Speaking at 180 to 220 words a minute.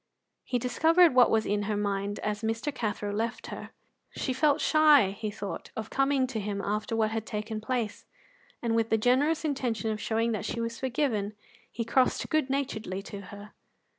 Yes: average, 185 wpm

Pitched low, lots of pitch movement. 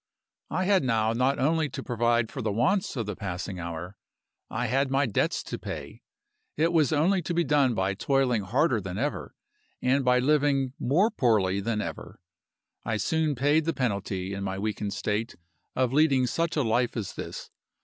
Yes: low, 125 Hz; wide, 5.7 semitones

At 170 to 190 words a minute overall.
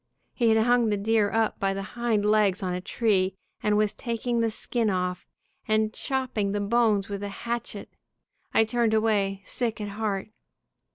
Yes: average, 180 wpm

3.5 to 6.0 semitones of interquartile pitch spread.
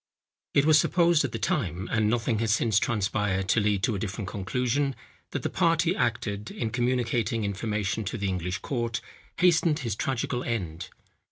Yes: average, 3.9 semitones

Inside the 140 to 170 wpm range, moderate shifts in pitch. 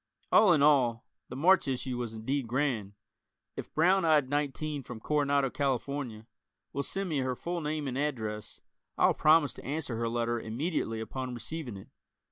Yes: average, 165 wpm; average, 4.1 semitones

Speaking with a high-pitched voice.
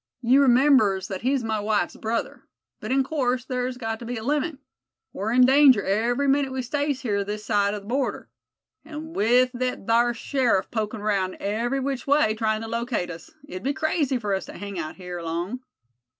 Yes: high, 240 Hz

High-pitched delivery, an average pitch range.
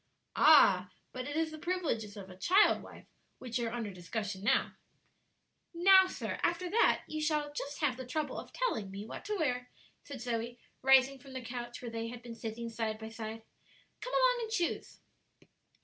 No: very high, 250 Hz; wide, 5.7 semitones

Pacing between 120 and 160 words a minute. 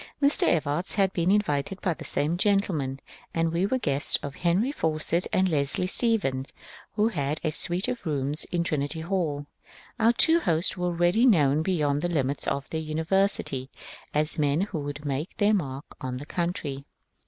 No: average, 175 wpm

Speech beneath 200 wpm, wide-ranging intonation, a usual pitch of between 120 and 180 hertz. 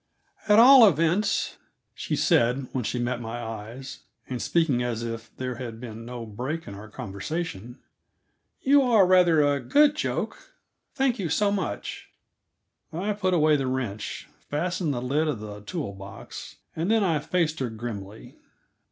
Yes: average, 160 wpm; wide, 7.6 semitones; low, 135 Hz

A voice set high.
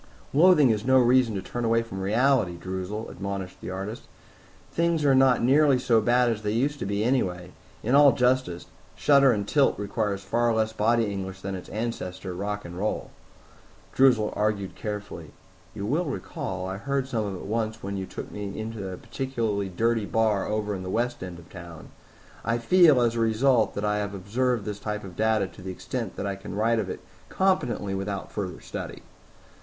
No: low, 110 Hz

